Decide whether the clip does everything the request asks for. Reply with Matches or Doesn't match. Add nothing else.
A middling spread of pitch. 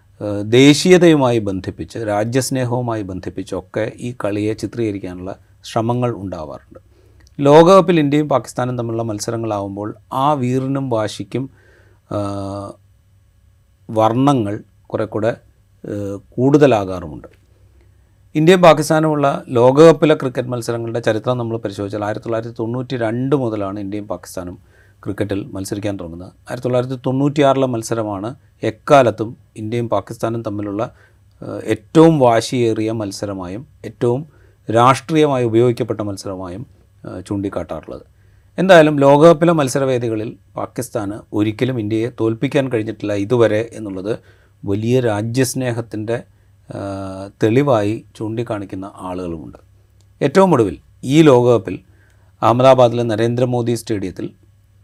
Matches